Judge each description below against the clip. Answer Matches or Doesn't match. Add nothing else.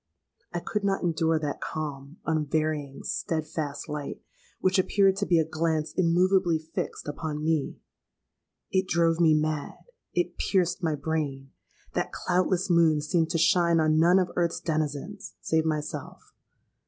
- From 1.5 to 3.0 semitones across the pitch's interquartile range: Matches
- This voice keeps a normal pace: Doesn't match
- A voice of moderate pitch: Matches